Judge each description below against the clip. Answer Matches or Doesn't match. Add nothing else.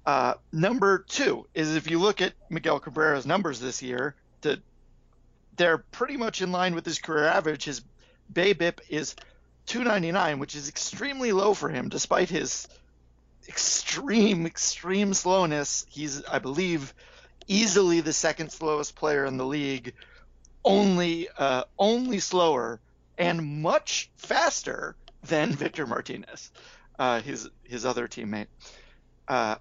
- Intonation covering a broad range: Matches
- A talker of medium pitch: Matches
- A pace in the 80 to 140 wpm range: Matches